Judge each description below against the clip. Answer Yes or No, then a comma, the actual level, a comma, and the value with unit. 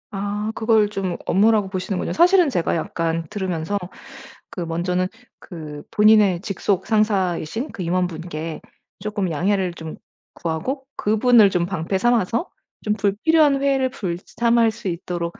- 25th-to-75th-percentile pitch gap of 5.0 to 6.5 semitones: No, average, 4.2 semitones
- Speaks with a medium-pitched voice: No, high, 195 Hz